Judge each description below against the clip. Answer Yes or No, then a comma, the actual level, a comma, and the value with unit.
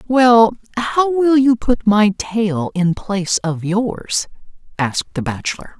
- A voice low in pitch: No, high, 215 Hz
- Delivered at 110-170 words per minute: Yes, average, 145 wpm